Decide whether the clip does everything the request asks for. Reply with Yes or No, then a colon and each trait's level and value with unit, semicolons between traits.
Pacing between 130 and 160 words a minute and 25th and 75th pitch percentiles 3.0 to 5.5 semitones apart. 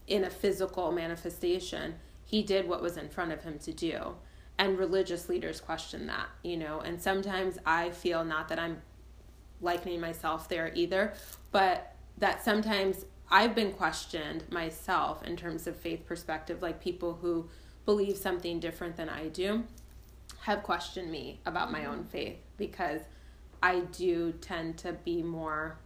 No: average, 155 wpm; narrow, 2.5 semitones